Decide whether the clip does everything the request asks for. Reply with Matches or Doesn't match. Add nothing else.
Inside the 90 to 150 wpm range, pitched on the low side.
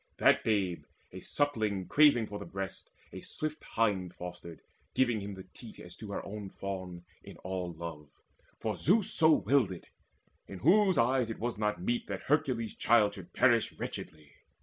Doesn't match